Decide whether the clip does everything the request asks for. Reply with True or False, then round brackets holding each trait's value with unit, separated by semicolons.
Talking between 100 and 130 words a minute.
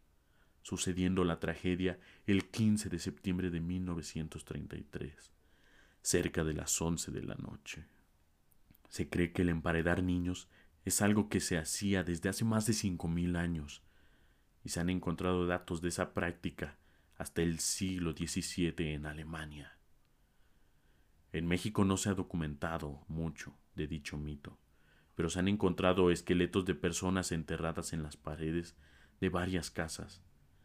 False (140 wpm)